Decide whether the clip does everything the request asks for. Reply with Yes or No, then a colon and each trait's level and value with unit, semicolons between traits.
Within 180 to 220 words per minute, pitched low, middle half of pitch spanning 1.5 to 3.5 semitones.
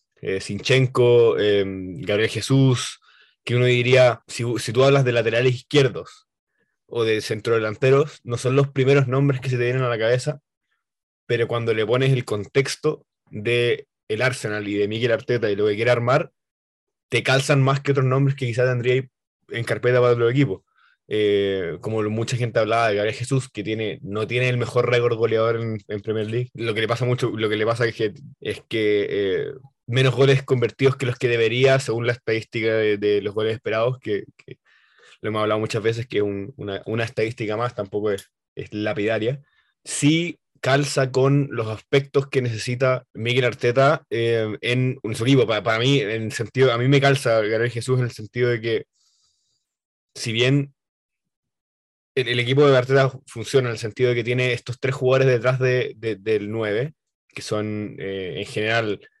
Yes: average, 185 wpm; low, 120 Hz; average, 3.1 semitones